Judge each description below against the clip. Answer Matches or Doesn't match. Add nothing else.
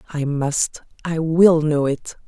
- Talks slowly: Matches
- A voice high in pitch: Doesn't match